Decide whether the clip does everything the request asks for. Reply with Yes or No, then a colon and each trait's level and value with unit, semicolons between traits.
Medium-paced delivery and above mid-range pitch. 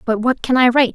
No: fast, 320 wpm; high, 245 Hz